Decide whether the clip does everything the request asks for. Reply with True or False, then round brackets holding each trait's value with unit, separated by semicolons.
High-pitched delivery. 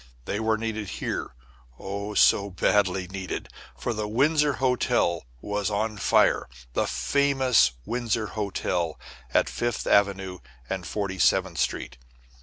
False (105 Hz)